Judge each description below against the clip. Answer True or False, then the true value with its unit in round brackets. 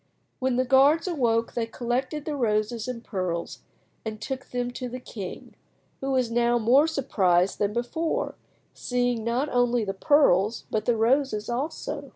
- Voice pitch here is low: False (245 Hz)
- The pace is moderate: True (160 wpm)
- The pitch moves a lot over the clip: False (3.3 semitones)